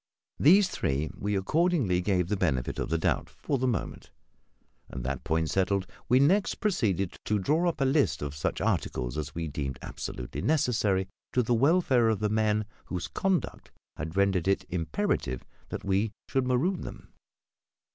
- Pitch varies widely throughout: Yes, wide, 8.2 semitones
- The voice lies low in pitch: Yes, low, 100 Hz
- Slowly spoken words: No, average, 165 wpm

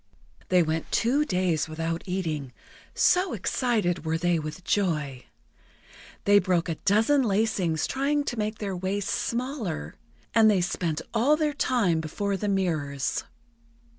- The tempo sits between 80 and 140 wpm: Yes, slow, 135 wpm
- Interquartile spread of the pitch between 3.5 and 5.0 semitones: No, wide, 5.5 semitones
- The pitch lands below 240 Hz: Yes, medium, 185 Hz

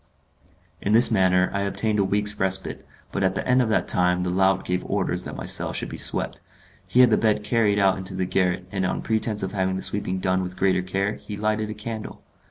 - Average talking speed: No, fast, 235 wpm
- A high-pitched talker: No, very low, 95 Hz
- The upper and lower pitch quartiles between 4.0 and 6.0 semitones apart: No, narrow, 2.4 semitones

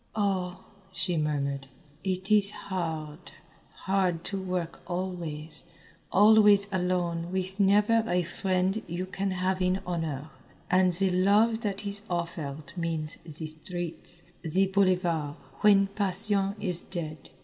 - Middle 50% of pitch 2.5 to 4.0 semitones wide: Yes, average, 2.8 semitones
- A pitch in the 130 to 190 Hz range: Yes, medium, 185 Hz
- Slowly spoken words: Yes, slow, 125 wpm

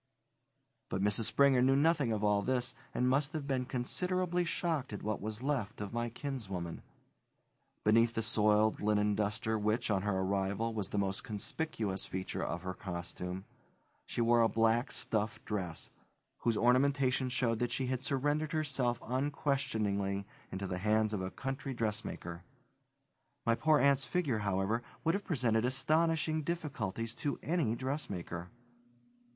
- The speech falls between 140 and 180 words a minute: Yes, average, 150 wpm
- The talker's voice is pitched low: Yes, low, 115 Hz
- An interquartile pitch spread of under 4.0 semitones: No, average, 4.9 semitones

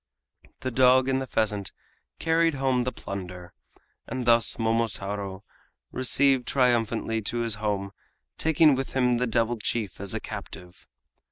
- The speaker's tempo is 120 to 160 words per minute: Yes, average, 140 wpm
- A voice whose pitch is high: No, low, 115 Hz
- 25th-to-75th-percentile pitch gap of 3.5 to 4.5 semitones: Yes, average, 4.0 semitones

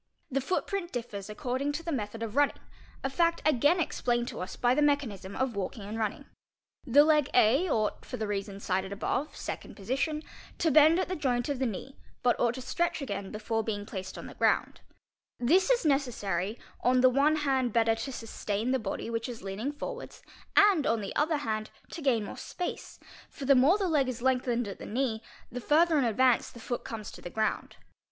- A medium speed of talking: No, fast, 215 wpm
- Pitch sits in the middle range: No, very high, 250 Hz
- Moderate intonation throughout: Yes, average, 5.0 semitones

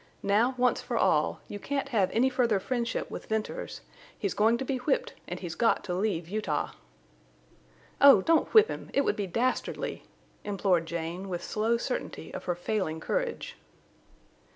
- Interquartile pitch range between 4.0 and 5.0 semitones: No, wide, 5.6 semitones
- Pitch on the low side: No, high, 215 Hz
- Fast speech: No, average, 165 wpm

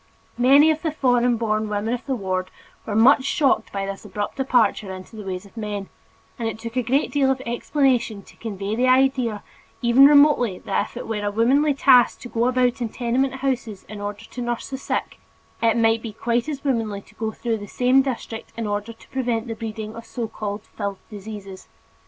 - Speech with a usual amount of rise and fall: Yes, average, 3.4 semitones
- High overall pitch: Yes, high, 230 Hz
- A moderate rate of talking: No, fast, 210 wpm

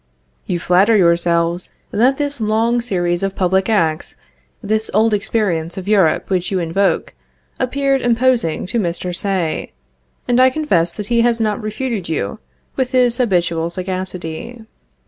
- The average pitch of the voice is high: Yes, high, 200 Hz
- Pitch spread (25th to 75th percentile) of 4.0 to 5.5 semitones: Yes, average, 5.2 semitones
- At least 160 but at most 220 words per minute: No, average, 145 wpm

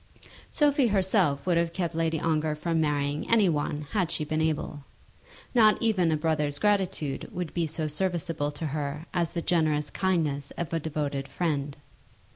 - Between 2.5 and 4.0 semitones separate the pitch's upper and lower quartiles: Yes, average, 3.1 semitones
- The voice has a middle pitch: Yes, medium, 160 Hz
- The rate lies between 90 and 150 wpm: No, average, 165 wpm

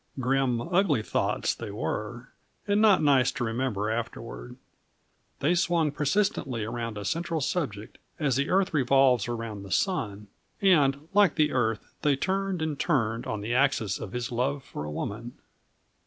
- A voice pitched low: Yes, low, 130 Hz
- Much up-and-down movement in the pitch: Yes, wide, 5.9 semitones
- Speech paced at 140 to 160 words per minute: Yes, average, 155 wpm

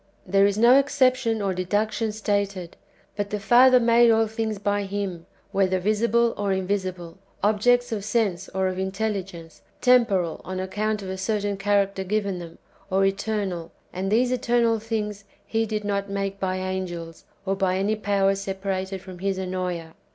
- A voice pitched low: No, high, 200 Hz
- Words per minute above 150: Yes, average, 170 wpm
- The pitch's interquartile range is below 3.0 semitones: Yes, narrow, 2.5 semitones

